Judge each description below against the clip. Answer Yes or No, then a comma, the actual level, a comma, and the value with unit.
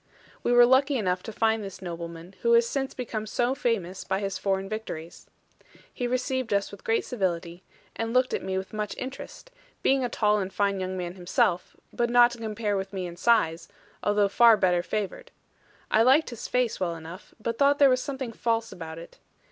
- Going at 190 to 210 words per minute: Yes, average, 200 wpm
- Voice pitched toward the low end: No, high, 215 Hz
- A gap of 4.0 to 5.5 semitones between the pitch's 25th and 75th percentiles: Yes, average, 4.4 semitones